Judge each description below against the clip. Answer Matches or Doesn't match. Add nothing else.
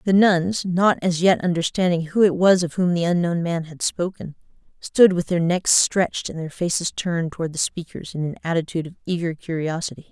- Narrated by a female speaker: Matches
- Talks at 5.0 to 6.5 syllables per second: Matches